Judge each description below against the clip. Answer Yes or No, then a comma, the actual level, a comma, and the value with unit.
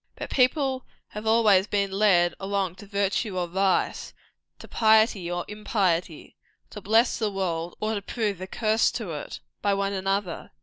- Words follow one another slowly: No, average, 165 wpm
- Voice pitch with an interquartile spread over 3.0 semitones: No, average, 2.7 semitones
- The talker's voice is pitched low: No, high, 200 Hz